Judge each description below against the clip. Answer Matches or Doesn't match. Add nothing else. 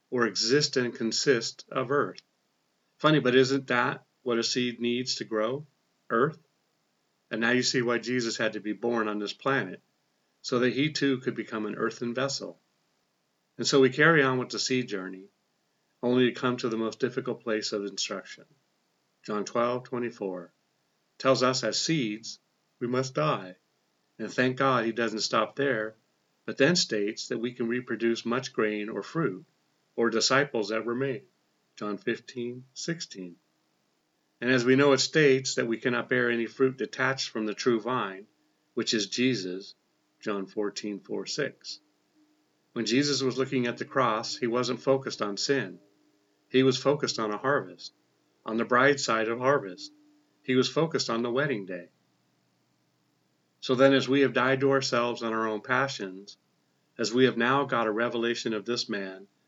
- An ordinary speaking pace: Matches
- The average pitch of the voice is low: Matches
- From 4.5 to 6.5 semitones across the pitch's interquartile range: Doesn't match